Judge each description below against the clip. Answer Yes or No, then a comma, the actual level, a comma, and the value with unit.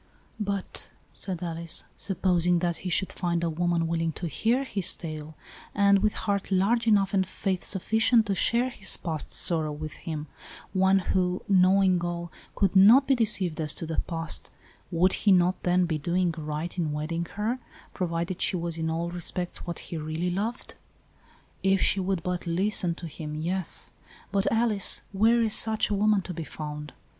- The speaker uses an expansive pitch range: No, average, 3.0 semitones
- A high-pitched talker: No, medium, 180 Hz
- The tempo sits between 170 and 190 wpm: Yes, average, 185 wpm